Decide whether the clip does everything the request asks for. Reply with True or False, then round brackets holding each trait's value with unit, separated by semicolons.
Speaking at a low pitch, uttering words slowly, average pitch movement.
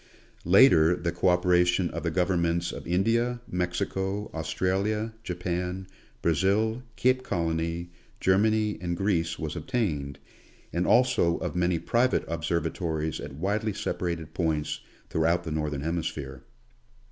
True (90 Hz; 120 wpm; 3.0 semitones)